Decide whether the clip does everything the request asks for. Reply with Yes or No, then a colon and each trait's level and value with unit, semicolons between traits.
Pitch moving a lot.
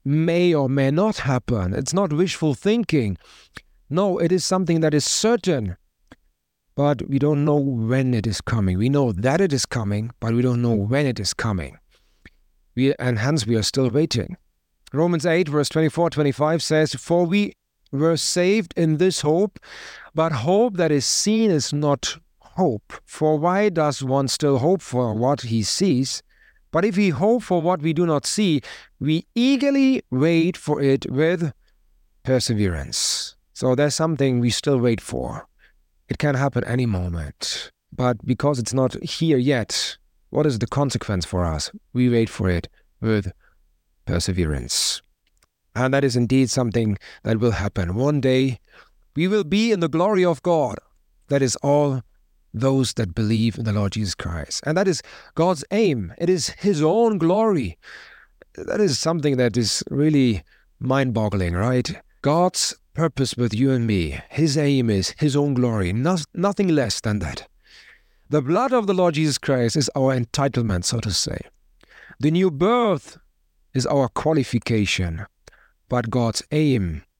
Yes: wide, 6.2 semitones